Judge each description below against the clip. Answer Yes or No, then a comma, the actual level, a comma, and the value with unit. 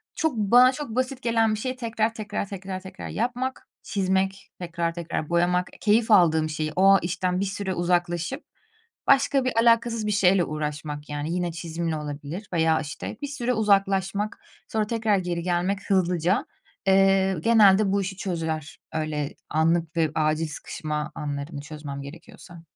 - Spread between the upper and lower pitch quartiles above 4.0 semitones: Yes, average, 4.7 semitones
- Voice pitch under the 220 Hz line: Yes, medium, 185 Hz